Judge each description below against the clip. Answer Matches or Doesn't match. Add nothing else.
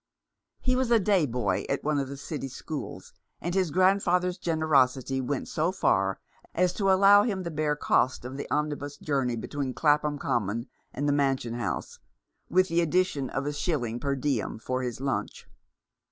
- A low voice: Doesn't match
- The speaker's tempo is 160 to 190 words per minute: Matches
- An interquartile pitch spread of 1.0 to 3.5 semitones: Doesn't match